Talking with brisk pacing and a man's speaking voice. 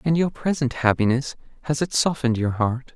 No: average, 185 wpm; male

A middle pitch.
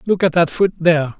Yes: medium, 170 Hz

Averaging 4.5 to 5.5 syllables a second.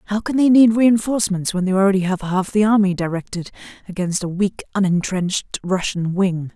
No: 5.7 syllables/s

